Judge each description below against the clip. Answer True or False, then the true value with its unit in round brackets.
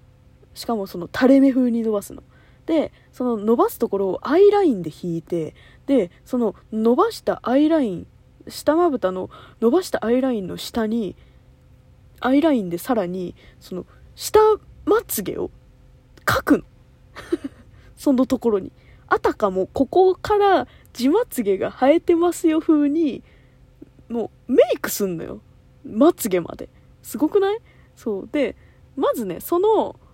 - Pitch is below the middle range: False (260 Hz)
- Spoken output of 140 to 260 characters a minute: False (270 characters per minute)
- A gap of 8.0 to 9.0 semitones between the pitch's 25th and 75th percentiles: False (7.4 semitones)